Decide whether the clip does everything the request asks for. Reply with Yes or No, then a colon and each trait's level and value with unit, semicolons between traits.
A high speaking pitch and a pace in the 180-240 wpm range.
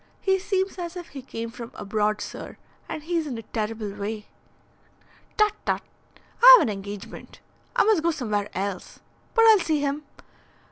No: very high, 270 Hz; average, 170 wpm